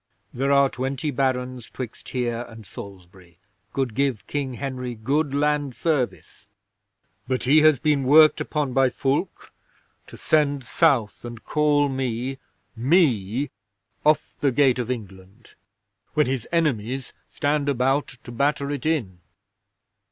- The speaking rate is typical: No, slow, 130 wpm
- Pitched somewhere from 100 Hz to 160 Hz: Yes, low, 135 Hz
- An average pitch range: Yes, average, 3.3 semitones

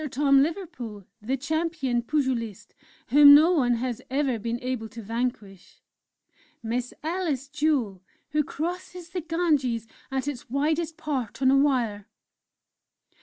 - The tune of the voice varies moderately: Yes, average, 4.5 semitones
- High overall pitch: Yes, very high, 270 Hz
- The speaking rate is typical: No, slow, 125 wpm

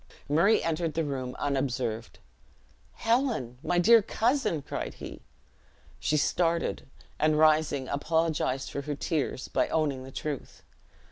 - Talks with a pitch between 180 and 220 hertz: No, medium, 150 Hz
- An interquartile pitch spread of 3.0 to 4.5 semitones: Yes, average, 3.7 semitones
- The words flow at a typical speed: No, slow, 125 wpm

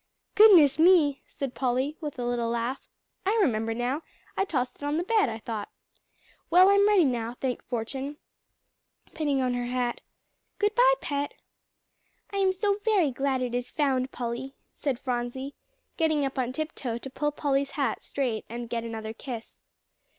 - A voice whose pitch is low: No, very high, 270 Hz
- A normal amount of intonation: Yes, average, 4.3 semitones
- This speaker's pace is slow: No, average, 165 wpm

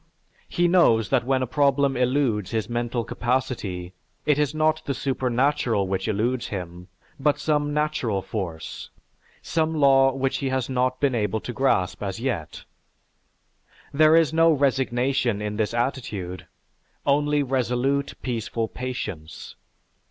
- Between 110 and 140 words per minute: Yes, slow, 135 wpm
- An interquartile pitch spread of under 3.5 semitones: No, average, 4.2 semitones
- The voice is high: No, low, 130 Hz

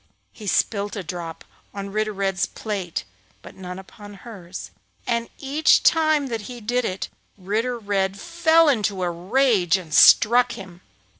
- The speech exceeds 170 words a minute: No, average, 150 wpm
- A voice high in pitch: Yes, high, 205 Hz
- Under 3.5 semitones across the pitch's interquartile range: No, average, 4.3 semitones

